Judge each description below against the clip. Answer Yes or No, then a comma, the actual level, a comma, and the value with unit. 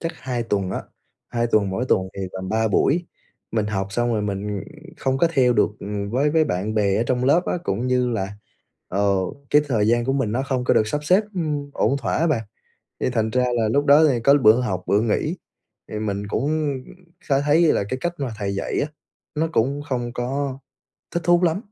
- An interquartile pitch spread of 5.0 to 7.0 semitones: Yes, average, 5.3 semitones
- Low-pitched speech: Yes, low, 125 Hz